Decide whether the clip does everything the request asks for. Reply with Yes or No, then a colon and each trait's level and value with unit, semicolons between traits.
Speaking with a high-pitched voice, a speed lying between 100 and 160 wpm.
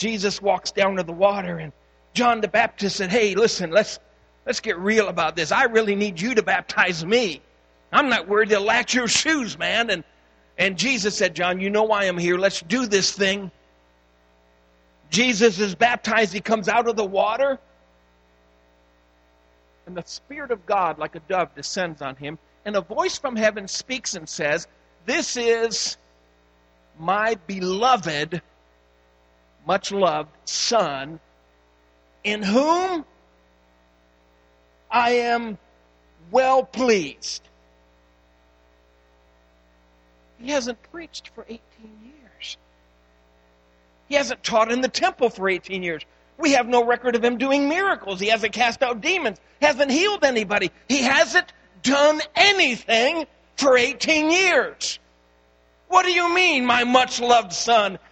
Yes: high, 195 Hz; average, 140 wpm